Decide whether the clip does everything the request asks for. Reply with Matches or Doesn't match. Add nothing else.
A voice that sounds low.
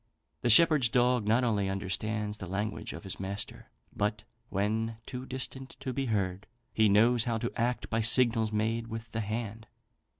Matches